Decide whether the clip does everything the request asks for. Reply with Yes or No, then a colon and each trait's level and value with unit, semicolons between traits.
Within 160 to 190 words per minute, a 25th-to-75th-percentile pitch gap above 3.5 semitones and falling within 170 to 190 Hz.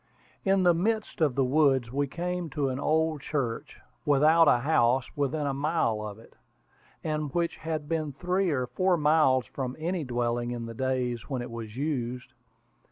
No: average, 175 wpm; average, 4.3 semitones; medium, 140 Hz